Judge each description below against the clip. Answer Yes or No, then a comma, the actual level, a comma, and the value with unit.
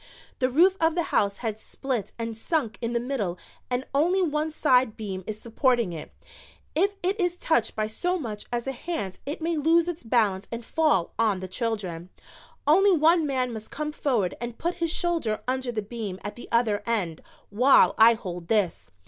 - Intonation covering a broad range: Yes, wide, 6.6 semitones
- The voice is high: Yes, high, 240 Hz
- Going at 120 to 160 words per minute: No, average, 190 wpm